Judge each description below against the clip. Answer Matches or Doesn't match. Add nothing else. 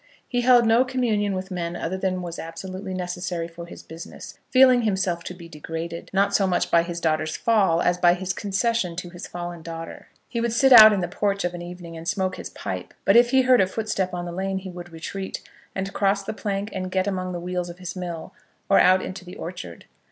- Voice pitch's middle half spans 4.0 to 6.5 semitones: Doesn't match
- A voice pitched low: Doesn't match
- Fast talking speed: Matches